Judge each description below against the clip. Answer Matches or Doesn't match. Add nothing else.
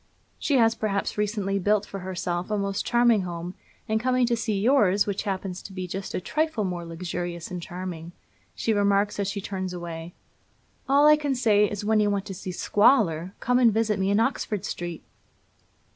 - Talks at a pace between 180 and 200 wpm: Matches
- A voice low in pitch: Doesn't match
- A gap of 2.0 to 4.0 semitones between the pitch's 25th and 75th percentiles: Matches